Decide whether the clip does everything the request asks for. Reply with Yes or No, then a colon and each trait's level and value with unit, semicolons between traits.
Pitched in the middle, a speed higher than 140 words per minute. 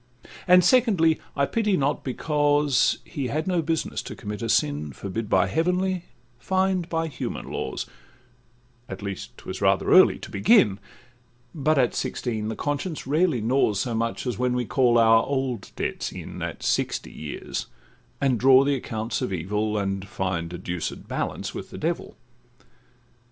No: low, 125 Hz; average, 160 wpm